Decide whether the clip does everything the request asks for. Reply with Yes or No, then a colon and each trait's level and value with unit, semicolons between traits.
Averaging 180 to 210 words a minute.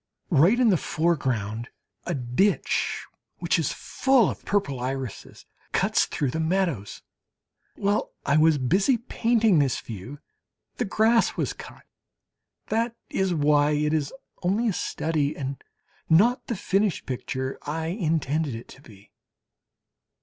No: slow, 135 wpm